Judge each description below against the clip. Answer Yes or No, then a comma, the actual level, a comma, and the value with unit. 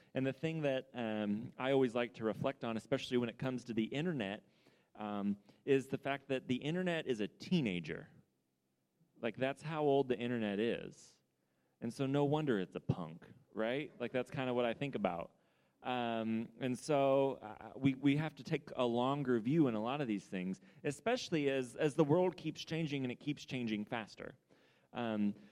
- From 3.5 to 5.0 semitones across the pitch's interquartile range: Yes, average, 3.9 semitones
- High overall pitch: No, low, 130 Hz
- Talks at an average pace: Yes, average, 195 wpm